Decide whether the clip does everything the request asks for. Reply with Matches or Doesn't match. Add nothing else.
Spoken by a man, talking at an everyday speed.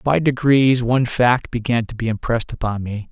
Matches